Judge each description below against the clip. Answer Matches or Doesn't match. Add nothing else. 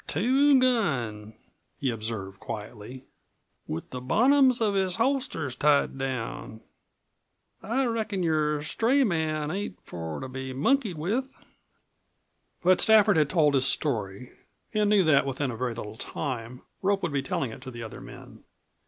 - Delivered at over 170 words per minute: Doesn't match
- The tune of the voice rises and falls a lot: Matches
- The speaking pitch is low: Doesn't match